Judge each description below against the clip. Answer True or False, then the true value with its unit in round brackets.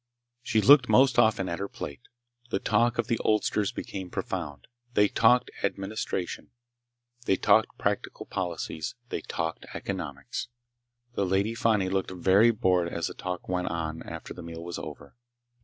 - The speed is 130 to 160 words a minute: True (155 wpm)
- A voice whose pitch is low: True (95 Hz)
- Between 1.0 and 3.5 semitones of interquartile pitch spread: False (4.3 semitones)